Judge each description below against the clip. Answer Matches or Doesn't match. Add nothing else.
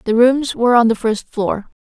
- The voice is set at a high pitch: Matches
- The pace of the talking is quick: Matches